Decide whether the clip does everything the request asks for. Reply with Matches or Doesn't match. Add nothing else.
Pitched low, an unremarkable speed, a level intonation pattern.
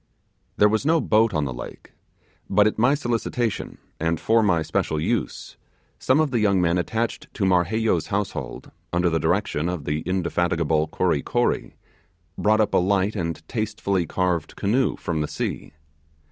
Doesn't match